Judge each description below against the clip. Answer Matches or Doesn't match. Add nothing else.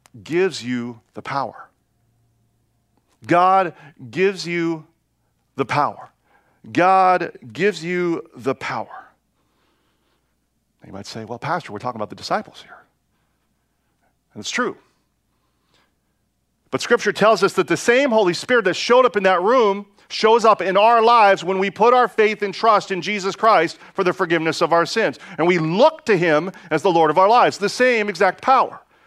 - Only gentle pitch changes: Doesn't match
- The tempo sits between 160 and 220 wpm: Matches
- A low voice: Doesn't match